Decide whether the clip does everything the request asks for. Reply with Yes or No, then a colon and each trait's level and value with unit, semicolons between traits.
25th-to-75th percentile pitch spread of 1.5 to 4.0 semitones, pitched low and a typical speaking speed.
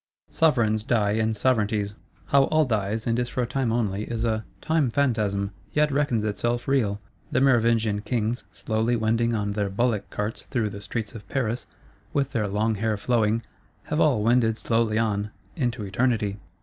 Yes: average, 2.7 semitones; low, 115 Hz; average, 165 wpm